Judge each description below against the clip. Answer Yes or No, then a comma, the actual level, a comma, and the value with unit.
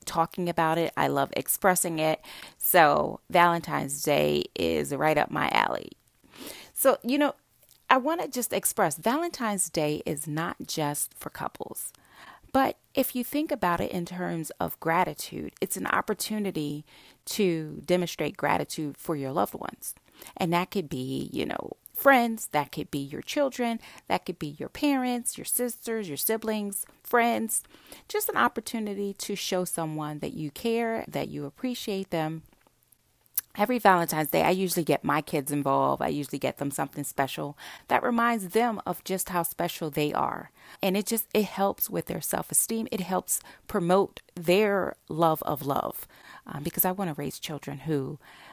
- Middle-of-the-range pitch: Yes, medium, 180 Hz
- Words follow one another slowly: No, average, 165 wpm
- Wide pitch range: Yes, wide, 6.8 semitones